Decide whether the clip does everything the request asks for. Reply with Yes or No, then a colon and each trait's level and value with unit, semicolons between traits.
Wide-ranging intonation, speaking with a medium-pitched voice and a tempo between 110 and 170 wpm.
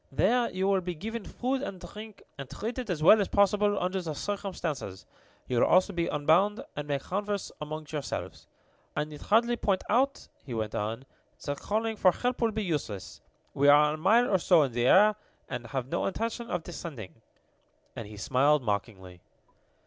No: wide, 6.8 semitones; medium, 180 Hz; average, 185 wpm